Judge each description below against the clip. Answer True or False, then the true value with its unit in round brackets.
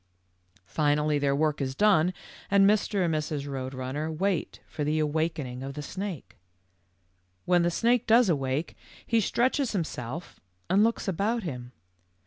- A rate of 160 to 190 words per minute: False (145 wpm)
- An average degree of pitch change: False (5.8 semitones)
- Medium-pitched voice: True (160 Hz)